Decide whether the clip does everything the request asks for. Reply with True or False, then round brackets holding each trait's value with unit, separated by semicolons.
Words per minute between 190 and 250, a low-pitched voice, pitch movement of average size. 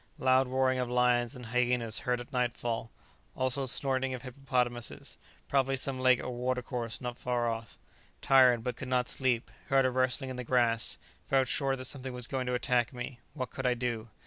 False (195 wpm; 125 Hz; 1.3 semitones)